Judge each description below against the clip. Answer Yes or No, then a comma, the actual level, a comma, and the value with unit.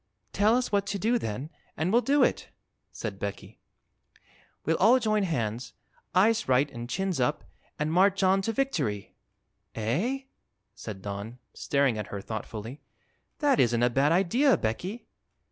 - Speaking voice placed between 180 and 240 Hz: No, medium, 165 Hz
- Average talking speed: Yes, average, 150 wpm